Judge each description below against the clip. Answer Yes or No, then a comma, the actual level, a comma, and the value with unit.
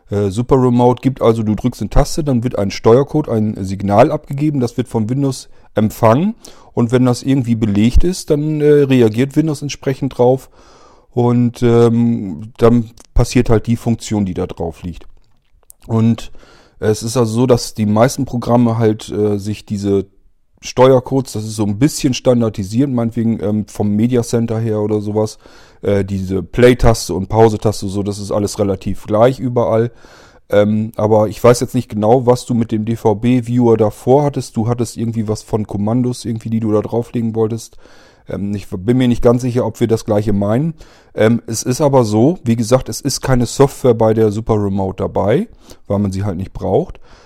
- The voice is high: No, low, 115 Hz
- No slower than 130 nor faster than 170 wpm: No, average, 180 wpm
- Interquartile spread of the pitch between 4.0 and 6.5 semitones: No, average, 2.8 semitones